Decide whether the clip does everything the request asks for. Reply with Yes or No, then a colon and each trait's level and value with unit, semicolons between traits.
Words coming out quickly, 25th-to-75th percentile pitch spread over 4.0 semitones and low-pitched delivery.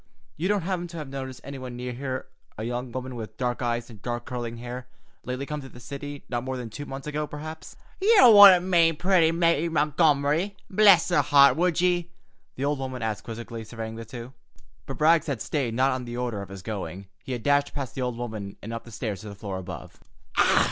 Yes: fast, 215 wpm; average, 4.6 semitones; low, 130 Hz